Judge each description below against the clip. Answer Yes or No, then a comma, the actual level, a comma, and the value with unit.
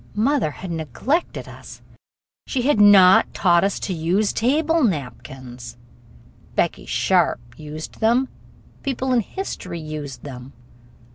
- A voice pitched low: No, medium, 185 Hz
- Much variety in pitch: Yes, wide, 8.6 semitones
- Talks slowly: Yes, slow, 120 wpm